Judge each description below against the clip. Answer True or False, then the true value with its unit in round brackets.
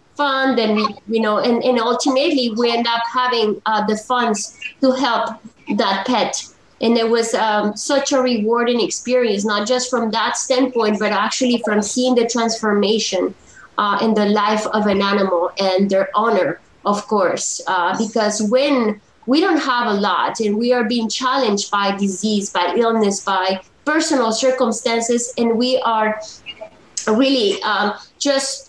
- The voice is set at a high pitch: True (230 Hz)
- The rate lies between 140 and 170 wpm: True (160 wpm)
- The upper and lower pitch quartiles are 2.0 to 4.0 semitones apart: True (3.1 semitones)